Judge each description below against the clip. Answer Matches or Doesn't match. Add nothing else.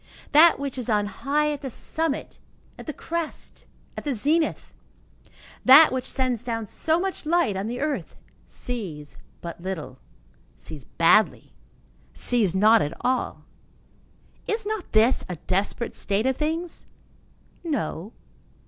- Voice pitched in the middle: Doesn't match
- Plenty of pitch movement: Matches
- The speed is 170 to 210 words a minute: Doesn't match